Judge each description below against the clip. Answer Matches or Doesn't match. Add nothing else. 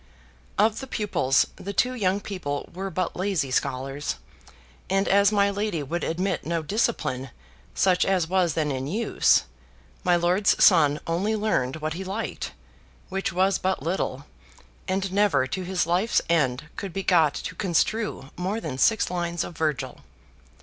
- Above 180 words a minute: Doesn't match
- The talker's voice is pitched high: Doesn't match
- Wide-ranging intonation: Doesn't match